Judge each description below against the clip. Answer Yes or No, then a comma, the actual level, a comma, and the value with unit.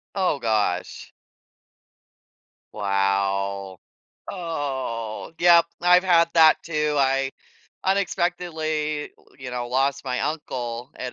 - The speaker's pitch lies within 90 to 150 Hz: Yes, medium, 140 Hz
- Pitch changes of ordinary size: No, wide, 6.2 semitones